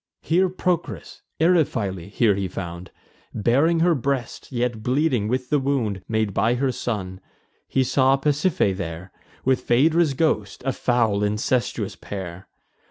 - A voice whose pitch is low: Yes, low, 120 Hz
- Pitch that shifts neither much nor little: No, wide, 5.7 semitones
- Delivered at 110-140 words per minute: Yes, slow, 135 wpm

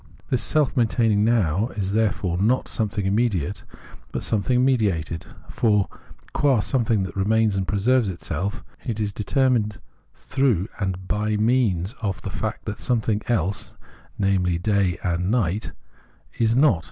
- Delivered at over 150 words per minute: No, average, 145 wpm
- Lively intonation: No, average, 3.4 semitones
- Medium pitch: No, low, 105 Hz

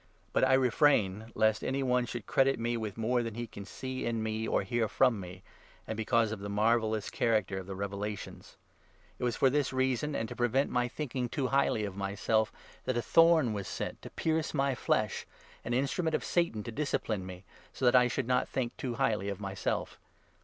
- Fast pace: Yes, fast, 215 wpm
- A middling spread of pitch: Yes, average, 3.6 semitones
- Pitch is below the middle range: Yes, low, 115 Hz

